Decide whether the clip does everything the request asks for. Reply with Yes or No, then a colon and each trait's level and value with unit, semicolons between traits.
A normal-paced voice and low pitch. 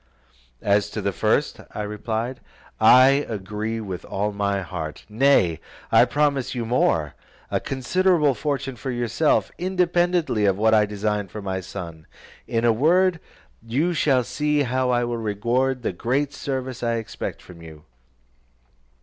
Yes: average, 150 wpm; low, 120 Hz